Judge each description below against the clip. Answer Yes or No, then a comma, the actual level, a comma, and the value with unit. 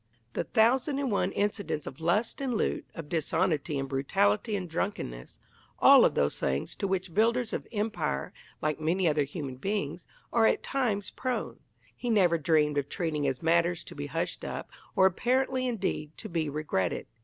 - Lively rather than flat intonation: Yes, wide, 6.3 semitones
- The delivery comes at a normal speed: Yes, average, 175 wpm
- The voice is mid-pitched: Yes, medium, 175 Hz